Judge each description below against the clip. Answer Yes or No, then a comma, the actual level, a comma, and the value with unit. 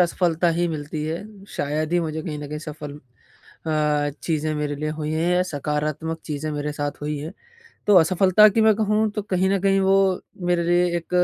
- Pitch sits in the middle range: Yes, medium, 160 Hz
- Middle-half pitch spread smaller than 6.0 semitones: Yes, average, 3.3 semitones